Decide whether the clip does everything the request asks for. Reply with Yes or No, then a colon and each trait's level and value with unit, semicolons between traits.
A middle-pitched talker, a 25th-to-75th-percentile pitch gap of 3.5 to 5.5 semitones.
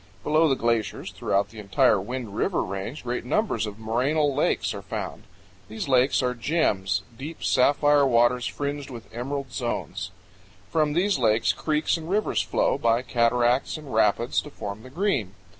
No: low, 125 Hz; average, 4.7 semitones